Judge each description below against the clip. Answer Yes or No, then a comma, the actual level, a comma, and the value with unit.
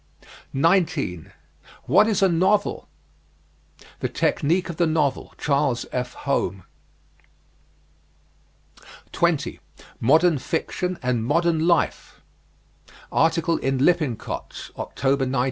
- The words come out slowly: Yes, slow, 95 wpm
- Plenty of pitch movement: No, average, 4.3 semitones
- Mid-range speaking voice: Yes, medium, 155 Hz